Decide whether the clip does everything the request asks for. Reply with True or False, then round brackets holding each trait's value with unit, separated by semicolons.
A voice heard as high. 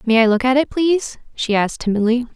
True (245 Hz)